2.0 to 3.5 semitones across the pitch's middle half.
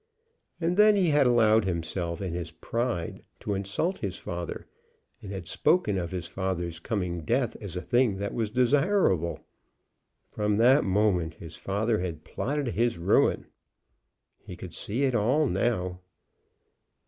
No: wide, 5.6 semitones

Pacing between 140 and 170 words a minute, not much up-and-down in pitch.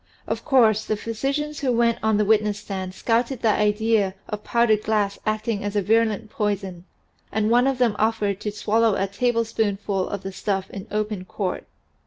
No: average, 180 wpm; narrow, 2.1 semitones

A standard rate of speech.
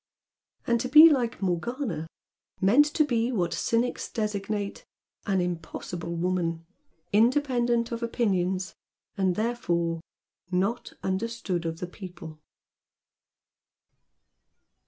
No: slow, 100 wpm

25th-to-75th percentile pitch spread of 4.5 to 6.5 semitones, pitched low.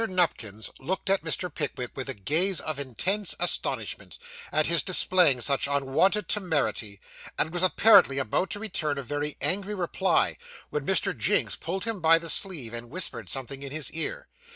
No: wide, 5.6 semitones; medium, 160 Hz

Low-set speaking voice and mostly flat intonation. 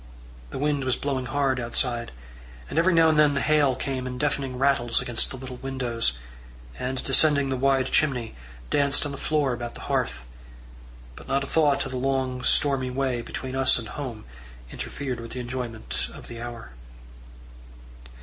Yes: low, 130 Hz; narrow, 2.2 semitones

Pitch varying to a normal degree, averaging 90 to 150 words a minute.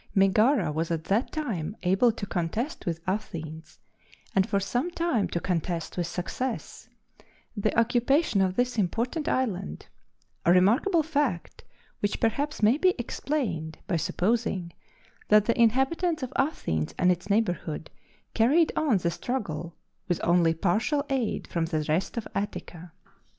No: wide, 6.6 semitones; average, 140 wpm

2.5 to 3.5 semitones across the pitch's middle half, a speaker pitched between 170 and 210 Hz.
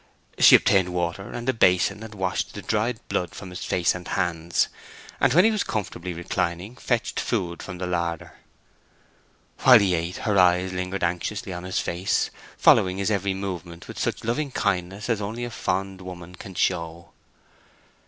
No: average, 3.1 semitones; very low, 95 Hz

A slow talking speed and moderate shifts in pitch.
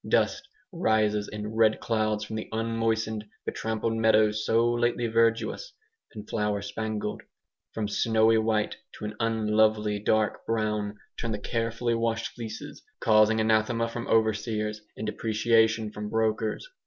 No: slow, 130 wpm; narrow, 1.1 semitones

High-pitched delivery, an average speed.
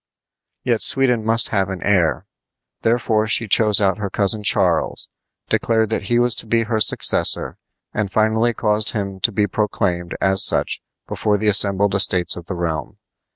No: low, 105 Hz; average, 165 wpm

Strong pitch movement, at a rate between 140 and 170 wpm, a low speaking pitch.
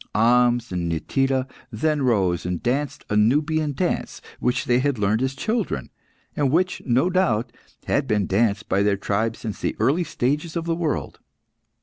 Yes: wide, 5.9 semitones; average, 165 wpm; low, 125 Hz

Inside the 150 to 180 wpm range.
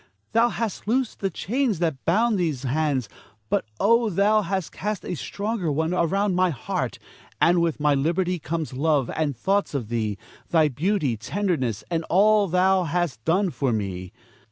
Yes: average, 165 wpm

